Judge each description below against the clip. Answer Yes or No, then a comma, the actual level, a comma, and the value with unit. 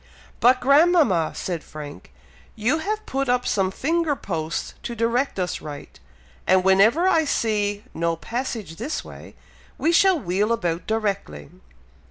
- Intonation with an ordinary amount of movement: No, wide, 7.6 semitones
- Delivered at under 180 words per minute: Yes, average, 140 wpm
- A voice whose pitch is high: Yes, high, 220 Hz